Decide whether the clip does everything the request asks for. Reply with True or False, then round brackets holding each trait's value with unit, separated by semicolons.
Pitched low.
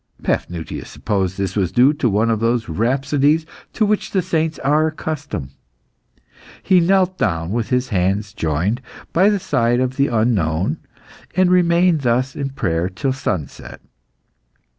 True (125 Hz)